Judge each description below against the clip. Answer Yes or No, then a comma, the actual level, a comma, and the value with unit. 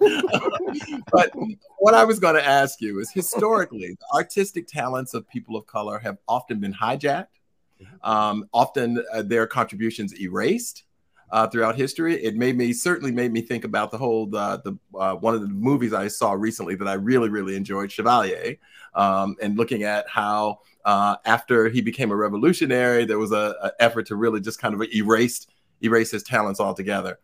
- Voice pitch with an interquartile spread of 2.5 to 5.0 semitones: Yes, average, 2.9 semitones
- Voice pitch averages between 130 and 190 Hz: No, low, 115 Hz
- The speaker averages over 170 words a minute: Yes, average, 180 wpm